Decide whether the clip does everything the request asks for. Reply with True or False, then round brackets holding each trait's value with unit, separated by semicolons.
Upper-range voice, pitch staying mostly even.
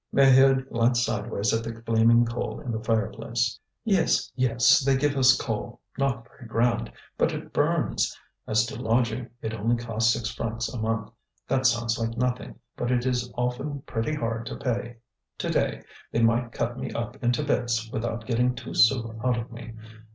False (120 Hz; 1.8 semitones)